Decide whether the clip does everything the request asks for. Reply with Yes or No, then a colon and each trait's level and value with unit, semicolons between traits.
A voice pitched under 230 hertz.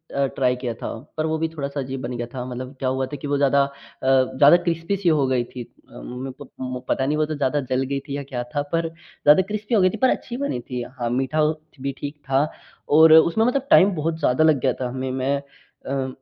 Yes: medium, 140 Hz